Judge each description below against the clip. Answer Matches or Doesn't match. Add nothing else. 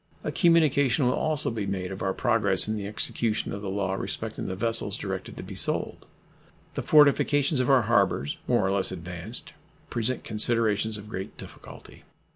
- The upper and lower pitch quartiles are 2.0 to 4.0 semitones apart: Doesn't match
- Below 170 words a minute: Doesn't match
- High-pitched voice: Doesn't match